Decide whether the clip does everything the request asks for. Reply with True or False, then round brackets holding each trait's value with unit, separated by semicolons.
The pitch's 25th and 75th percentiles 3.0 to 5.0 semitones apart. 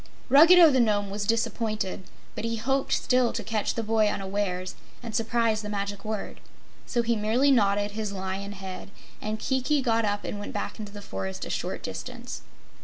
False (2.5 semitones)